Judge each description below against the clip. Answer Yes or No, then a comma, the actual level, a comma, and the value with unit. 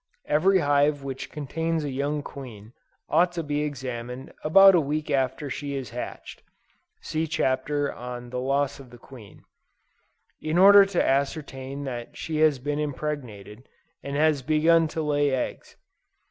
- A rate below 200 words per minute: Yes, average, 145 wpm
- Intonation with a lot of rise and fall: No, average, 2.8 semitones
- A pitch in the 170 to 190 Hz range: No, medium, 145 Hz